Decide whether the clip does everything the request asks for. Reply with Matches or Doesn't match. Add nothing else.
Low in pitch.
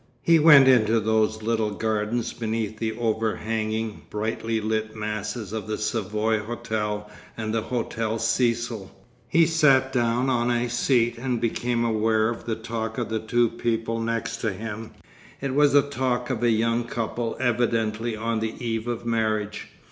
Matches